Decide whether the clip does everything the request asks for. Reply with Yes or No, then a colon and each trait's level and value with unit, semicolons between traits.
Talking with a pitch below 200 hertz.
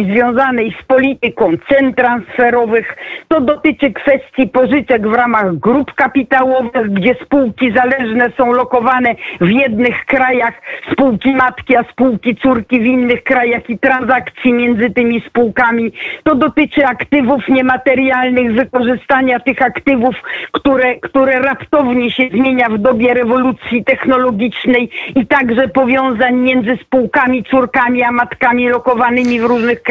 No: very high, 255 Hz